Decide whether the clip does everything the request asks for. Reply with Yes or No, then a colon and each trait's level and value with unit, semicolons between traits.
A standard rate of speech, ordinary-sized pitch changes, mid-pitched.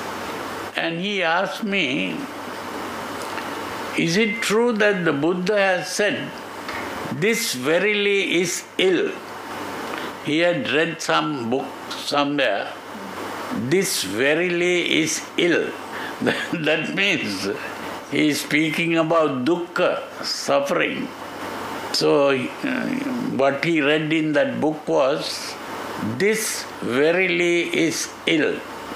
No: slow, 95 wpm; average, 4.9 semitones; medium, 175 Hz